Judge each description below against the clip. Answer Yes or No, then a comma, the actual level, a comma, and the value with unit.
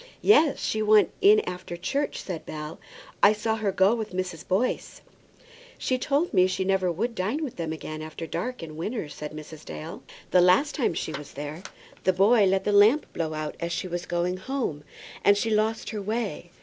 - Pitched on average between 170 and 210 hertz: Yes, high, 190 Hz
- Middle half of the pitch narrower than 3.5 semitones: No, average, 5.0 semitones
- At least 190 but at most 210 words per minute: Yes, average, 200 wpm